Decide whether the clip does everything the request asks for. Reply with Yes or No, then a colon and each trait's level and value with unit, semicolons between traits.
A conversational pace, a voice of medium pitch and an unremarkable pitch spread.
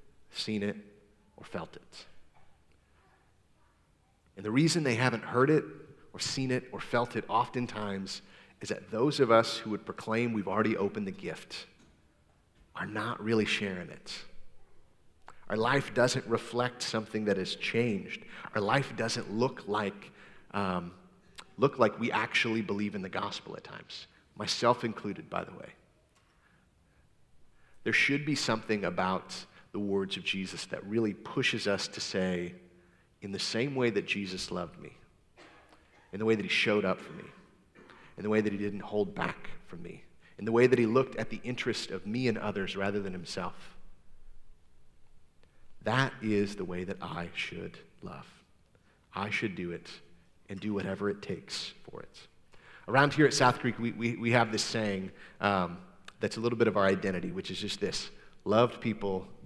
No: average, 170 wpm; low, 105 Hz; average, 3.6 semitones